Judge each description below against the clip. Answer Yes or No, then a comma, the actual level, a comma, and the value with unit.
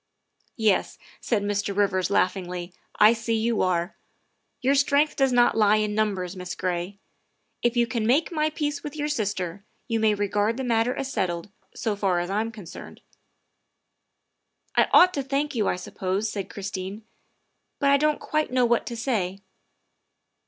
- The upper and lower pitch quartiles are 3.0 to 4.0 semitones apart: No, average, 4.7 semitones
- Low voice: No, high, 215 Hz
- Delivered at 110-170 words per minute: No, average, 190 wpm